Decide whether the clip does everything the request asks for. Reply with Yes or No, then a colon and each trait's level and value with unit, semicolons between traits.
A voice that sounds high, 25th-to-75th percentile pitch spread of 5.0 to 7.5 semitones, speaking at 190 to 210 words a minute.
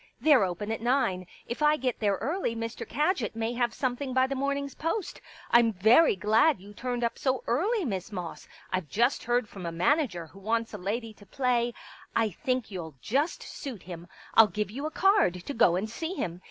Yes: high, 230 Hz; wide, 5.5 semitones; fast, 205 wpm